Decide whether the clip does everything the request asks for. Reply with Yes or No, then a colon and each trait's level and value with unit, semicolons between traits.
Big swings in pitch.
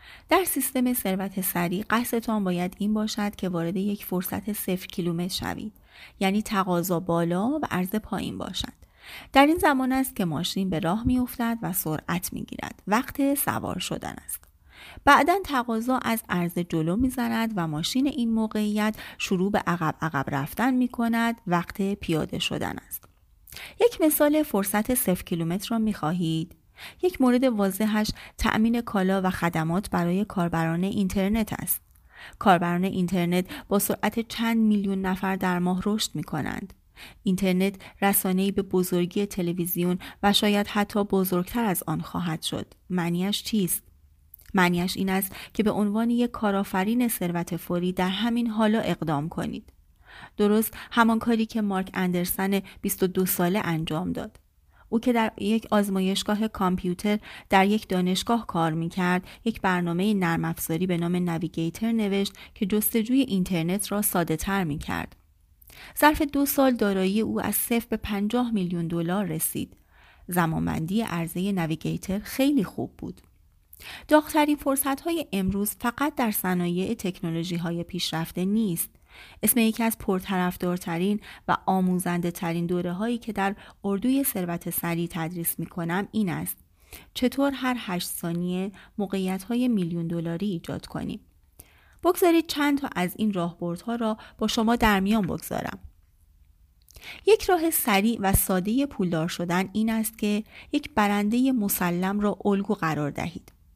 No: average, 4.3 semitones